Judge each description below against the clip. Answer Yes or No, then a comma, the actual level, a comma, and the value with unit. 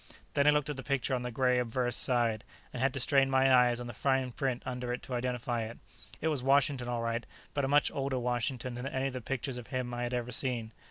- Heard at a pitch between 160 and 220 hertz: No, low, 125 Hz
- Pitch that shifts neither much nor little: No, narrow, 1.8 semitones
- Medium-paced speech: No, fast, 260 wpm